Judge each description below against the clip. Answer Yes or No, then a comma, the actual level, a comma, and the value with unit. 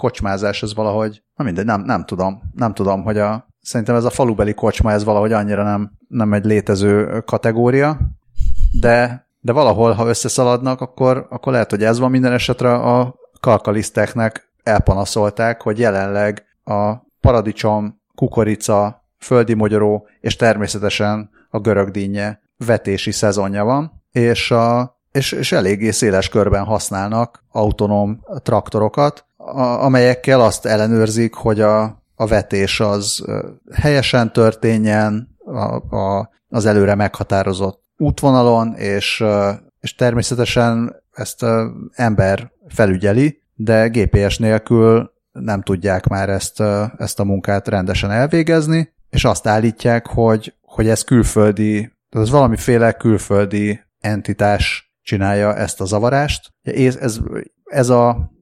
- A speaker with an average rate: Yes, average, 120 wpm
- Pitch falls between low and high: No, low, 110 Hz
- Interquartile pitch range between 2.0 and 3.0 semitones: Yes, average, 2.7 semitones